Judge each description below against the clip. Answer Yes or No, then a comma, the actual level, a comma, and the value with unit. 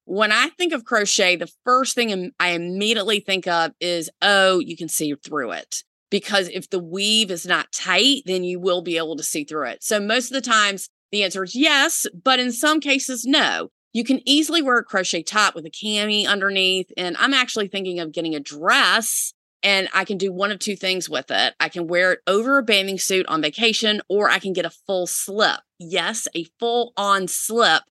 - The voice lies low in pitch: No, high, 195 Hz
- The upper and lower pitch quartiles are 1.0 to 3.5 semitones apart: No, average, 4.3 semitones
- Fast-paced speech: Yes, fast, 215 wpm